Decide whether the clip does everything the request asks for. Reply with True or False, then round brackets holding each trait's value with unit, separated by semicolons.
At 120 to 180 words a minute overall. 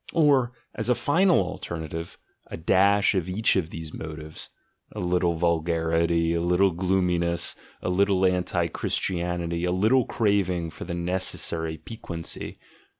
True (140 wpm)